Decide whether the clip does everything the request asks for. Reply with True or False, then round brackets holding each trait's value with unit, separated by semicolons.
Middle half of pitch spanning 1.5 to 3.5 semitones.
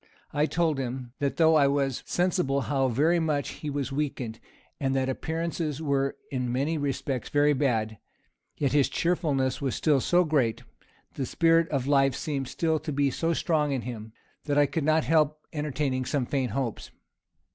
True (2.8 semitones)